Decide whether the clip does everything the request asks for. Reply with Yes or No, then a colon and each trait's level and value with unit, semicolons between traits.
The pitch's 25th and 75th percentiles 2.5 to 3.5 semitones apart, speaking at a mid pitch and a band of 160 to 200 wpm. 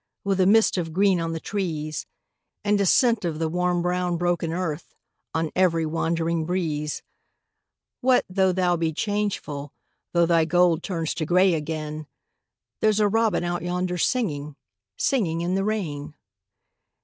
No: average, 2.9 semitones; medium, 175 Hz; average, 150 wpm